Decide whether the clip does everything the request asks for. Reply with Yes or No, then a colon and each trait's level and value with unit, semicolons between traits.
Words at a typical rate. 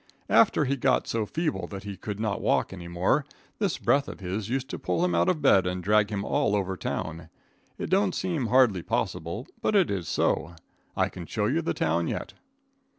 No: fast, 210 wpm